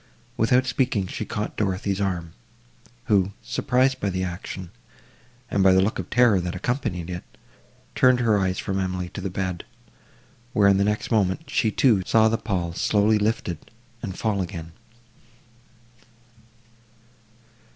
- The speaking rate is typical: Yes, average, 145 wpm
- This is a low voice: Yes, low, 100 Hz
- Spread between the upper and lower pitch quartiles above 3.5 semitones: No, average, 3.2 semitones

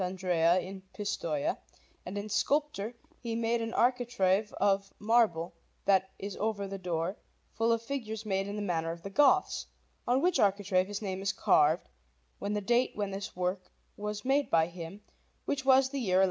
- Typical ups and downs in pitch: Yes, average, 3.7 semitones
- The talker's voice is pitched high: Yes, high, 200 Hz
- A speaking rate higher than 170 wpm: Yes, average, 180 wpm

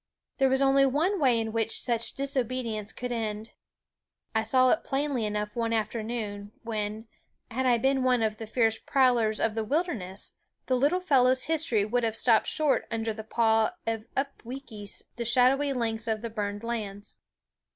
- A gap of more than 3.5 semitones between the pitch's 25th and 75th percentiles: No, average, 3.1 semitones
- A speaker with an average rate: Yes, average, 170 wpm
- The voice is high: Yes, high, 230 Hz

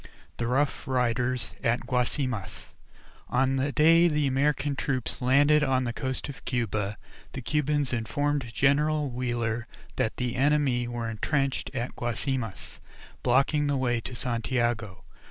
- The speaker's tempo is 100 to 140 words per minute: Yes, slow, 135 wpm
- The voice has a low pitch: Yes, low, 130 Hz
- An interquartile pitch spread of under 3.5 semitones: Yes, average, 3.1 semitones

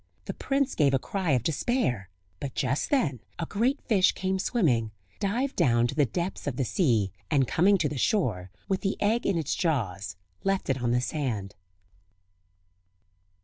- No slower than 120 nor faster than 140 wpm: No, average, 175 wpm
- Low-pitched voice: No, medium, 150 Hz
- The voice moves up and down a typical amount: No, wide, 8.1 semitones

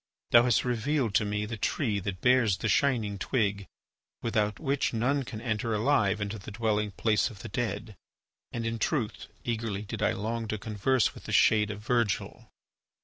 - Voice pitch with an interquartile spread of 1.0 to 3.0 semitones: Yes, narrow, 2.5 semitones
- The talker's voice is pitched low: Yes, low, 110 Hz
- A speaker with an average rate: Yes, average, 180 wpm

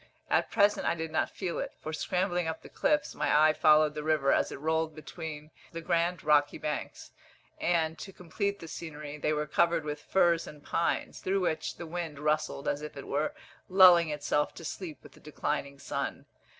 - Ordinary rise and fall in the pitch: No, narrow, 2.3 semitones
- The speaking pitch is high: No, medium, 160 Hz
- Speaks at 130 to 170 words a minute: No, average, 195 wpm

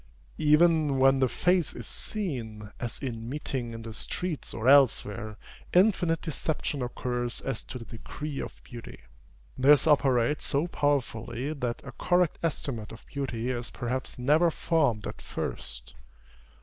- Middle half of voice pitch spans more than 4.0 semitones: Yes, average, 4.5 semitones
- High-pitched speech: No, low, 135 Hz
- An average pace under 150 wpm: Yes, average, 140 wpm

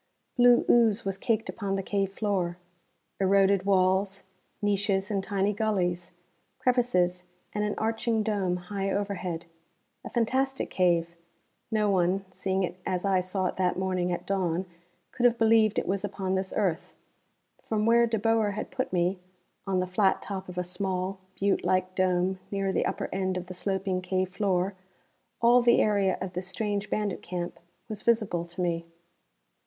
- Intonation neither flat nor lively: No, narrow, 2.3 semitones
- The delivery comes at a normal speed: Yes, average, 165 wpm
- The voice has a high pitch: Yes, high, 195 Hz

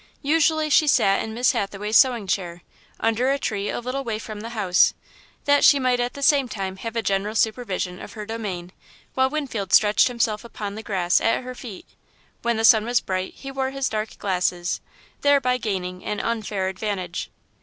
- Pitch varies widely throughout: No, average, 4.3 semitones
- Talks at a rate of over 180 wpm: Yes, average, 190 wpm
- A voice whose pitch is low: No, high, 220 Hz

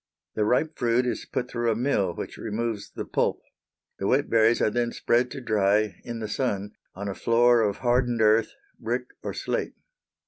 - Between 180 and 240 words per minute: Yes, average, 185 wpm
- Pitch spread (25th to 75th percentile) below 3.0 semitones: Yes, narrow, 2.5 semitones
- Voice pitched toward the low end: Yes, low, 115 Hz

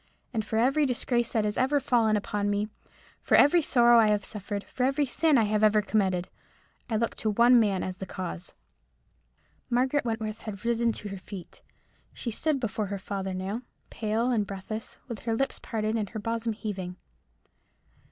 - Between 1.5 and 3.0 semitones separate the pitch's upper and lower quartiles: Yes, average, 2.7 semitones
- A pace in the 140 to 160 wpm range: No, average, 175 wpm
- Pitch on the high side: Yes, high, 220 Hz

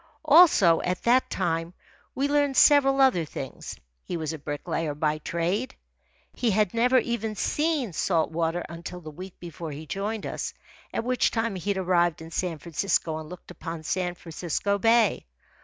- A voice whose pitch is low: No, medium, 180 Hz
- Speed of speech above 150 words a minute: Yes, average, 170 wpm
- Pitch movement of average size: No, wide, 5.8 semitones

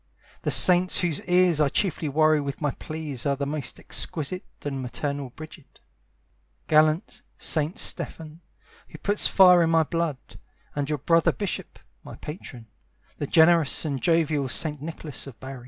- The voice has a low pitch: No, medium, 155 Hz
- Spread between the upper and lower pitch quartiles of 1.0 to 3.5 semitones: Yes, average, 2.9 semitones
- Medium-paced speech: Yes, average, 155 wpm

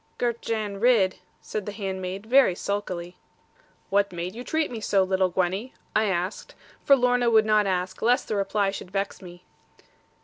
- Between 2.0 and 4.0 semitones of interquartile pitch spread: Yes, average, 3.3 semitones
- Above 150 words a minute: Yes, average, 170 wpm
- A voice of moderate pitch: No, high, 200 Hz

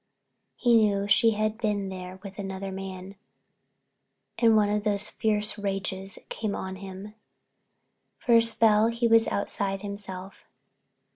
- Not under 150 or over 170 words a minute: No, average, 140 wpm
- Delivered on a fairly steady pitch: Yes, narrow, 2.0 semitones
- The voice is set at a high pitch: Yes, high, 205 Hz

